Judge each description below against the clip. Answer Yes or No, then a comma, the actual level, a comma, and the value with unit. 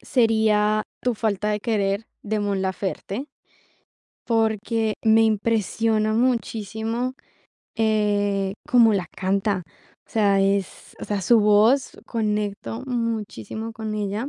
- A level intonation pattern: Yes, narrow, 1.8 semitones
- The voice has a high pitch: Yes, high, 215 Hz